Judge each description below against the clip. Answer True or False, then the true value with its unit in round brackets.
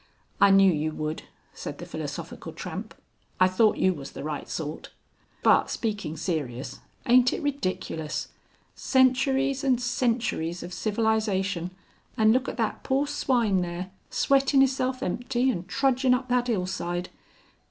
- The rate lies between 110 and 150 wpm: True (140 wpm)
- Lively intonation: True (6.4 semitones)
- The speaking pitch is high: True (220 Hz)